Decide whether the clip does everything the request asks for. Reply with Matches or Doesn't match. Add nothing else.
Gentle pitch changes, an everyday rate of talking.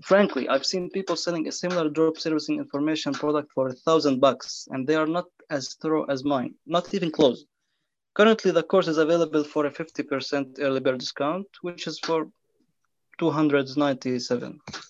Doesn't match